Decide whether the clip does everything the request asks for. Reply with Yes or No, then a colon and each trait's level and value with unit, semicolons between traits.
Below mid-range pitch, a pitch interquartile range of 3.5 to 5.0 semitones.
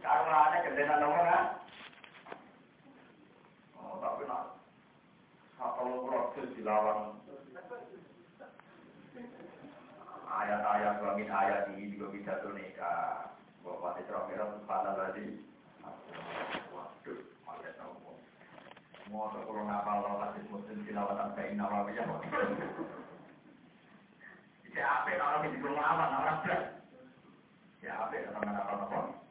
No: low, 105 Hz; wide, 5.5 semitones